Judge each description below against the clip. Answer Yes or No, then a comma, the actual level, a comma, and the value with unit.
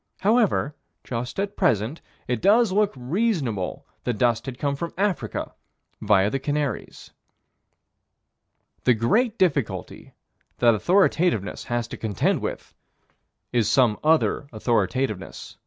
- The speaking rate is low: Yes, slow, 115 wpm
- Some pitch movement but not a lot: No, wide, 8.1 semitones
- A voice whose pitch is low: Yes, low, 130 Hz